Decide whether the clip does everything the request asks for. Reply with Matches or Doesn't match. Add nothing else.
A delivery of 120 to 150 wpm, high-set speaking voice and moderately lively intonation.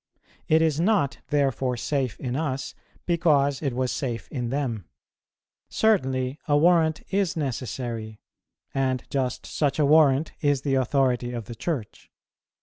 Doesn't match